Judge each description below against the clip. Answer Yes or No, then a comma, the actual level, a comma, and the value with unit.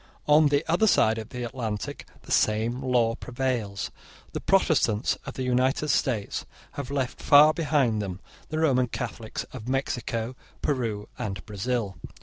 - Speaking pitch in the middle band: No, low, 125 Hz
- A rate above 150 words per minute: No, average, 145 wpm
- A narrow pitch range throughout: No, average, 3.6 semitones